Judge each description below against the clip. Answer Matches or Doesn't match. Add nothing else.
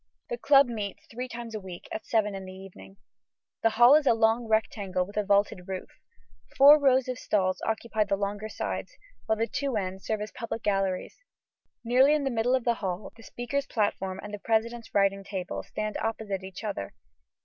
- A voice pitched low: Doesn't match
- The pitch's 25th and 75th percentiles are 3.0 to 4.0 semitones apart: Matches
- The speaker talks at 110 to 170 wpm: Doesn't match